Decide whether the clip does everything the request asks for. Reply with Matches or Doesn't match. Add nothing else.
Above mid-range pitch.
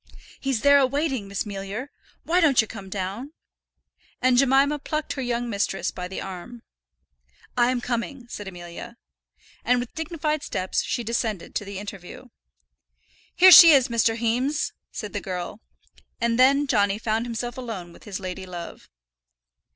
Matches